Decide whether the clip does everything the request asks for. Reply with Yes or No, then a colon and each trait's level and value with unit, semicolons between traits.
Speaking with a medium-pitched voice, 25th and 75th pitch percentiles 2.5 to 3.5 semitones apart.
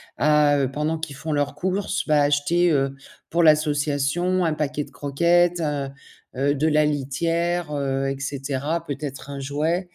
Yes: medium, 150 Hz; average, 2.9 semitones